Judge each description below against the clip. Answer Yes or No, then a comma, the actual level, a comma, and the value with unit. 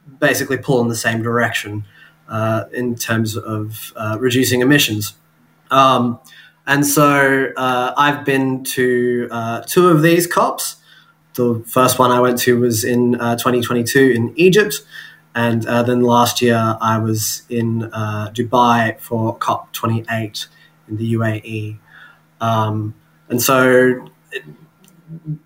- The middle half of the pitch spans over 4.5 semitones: No, average, 2.7 semitones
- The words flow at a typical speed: No, slow, 130 wpm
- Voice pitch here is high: No, low, 120 Hz